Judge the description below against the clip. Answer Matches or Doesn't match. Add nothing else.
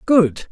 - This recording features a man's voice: Matches